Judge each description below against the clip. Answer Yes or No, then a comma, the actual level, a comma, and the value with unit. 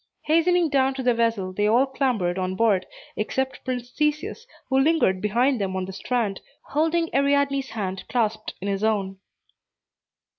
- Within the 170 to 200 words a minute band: No, average, 155 wpm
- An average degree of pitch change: No, wide, 5.9 semitones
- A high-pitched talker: Yes, high, 240 Hz